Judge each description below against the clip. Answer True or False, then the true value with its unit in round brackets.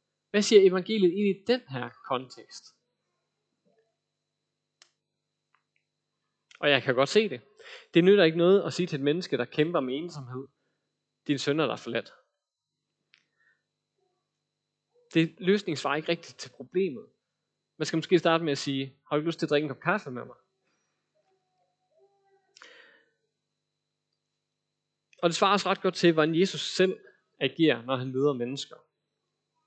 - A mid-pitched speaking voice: True (170 Hz)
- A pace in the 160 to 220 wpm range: False (150 wpm)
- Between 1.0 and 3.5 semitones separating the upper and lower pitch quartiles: False (5.3 semitones)